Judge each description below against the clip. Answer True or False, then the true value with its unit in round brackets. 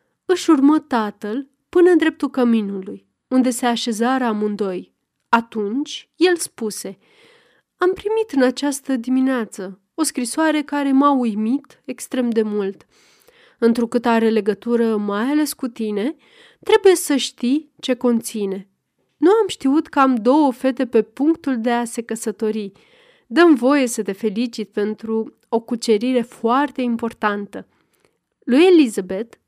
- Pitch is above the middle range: True (255 Hz)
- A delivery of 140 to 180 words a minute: False (130 wpm)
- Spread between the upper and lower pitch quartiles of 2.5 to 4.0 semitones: False (4.6 semitones)